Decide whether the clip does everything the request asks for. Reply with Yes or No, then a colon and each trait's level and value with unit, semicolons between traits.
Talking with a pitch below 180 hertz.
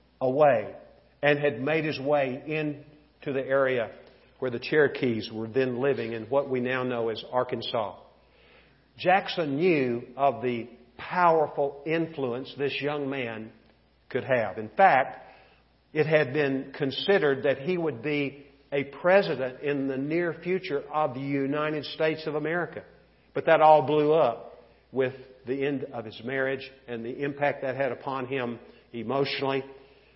Yes: medium, 140 Hz